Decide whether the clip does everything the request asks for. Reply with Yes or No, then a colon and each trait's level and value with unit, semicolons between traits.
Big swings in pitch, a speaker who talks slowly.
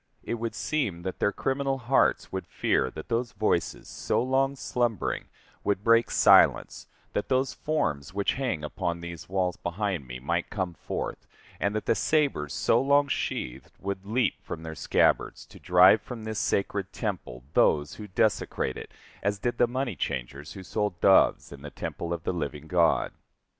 No: wide, 5.9 semitones; average, 175 wpm